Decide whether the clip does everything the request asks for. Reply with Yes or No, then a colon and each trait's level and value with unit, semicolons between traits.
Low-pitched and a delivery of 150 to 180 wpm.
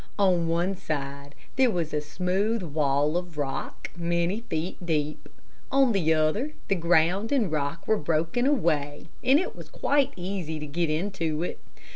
No: medium, 170 Hz; average, 160 wpm